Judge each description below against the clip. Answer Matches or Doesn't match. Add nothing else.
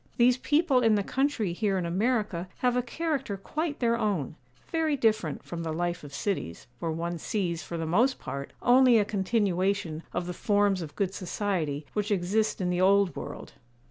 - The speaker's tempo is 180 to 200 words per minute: Matches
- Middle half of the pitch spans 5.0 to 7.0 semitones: Matches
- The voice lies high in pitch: Matches